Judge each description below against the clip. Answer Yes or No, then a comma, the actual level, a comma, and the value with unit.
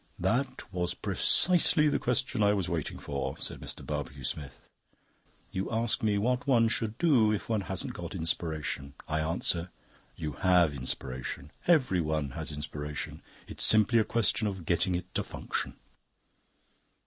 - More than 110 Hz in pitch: No, very low, 90 Hz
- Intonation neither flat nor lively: No, wide, 7.0 semitones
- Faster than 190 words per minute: No, average, 150 wpm